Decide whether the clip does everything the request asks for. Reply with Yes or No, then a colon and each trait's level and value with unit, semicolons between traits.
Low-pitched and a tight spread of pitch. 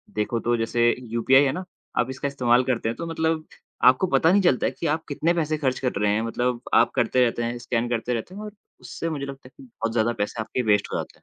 No: low, 125 Hz; average, 4.7 semitones